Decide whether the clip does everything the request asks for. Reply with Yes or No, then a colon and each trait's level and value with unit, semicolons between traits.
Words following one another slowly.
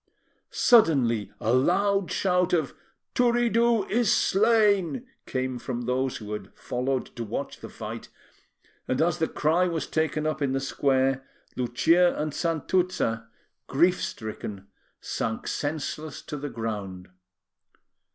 Yes: slow, 125 wpm